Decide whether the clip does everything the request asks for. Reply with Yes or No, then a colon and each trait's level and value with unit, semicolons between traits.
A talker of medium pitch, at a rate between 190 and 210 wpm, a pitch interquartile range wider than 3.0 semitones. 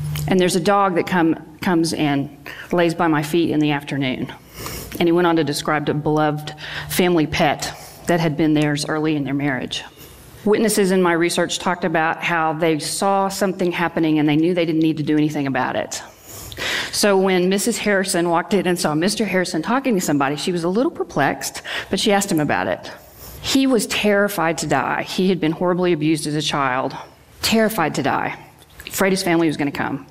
Yes: medium, 170 Hz; fast, 205 wpm; average, 3.7 semitones